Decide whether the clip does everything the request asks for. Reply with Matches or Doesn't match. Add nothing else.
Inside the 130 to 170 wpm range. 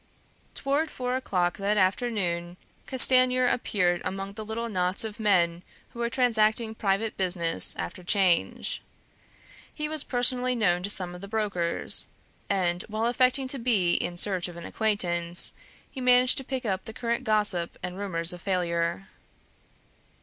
Matches